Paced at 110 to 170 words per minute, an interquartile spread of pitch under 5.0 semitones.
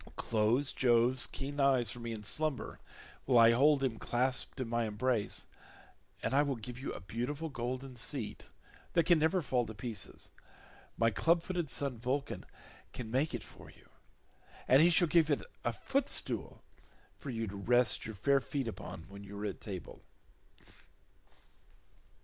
Yes: average, 160 wpm; average, 3.8 semitones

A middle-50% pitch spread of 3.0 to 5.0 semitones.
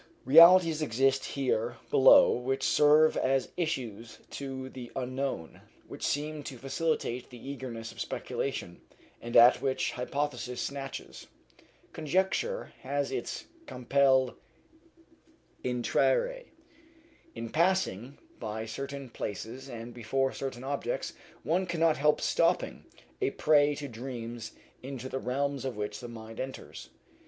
Yes: average, 3.4 semitones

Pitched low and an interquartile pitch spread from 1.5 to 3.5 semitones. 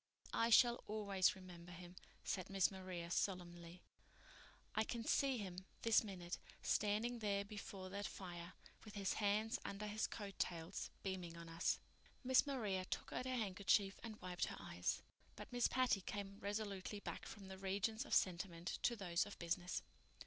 No: high, 195 Hz; average, 2.9 semitones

